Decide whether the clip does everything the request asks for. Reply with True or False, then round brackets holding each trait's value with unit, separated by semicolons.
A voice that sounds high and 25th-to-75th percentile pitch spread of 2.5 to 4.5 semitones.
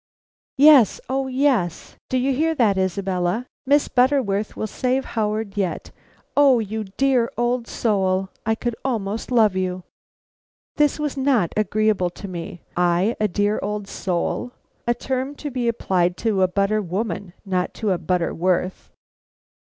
False (215 Hz; 5.2 semitones)